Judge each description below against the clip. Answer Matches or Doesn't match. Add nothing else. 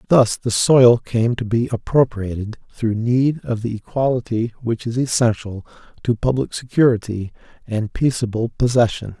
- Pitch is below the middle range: Matches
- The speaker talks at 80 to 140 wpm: Matches